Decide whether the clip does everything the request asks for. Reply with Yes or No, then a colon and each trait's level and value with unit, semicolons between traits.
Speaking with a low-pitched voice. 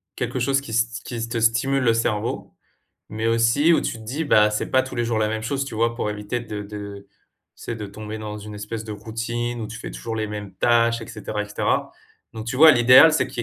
Yes: low, 115 Hz